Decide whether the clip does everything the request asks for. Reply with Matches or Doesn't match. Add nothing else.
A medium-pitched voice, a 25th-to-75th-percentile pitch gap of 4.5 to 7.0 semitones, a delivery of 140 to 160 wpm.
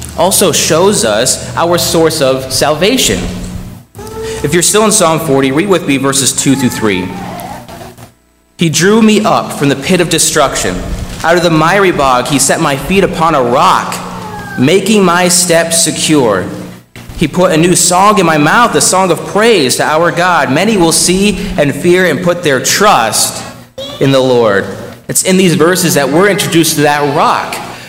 Doesn't match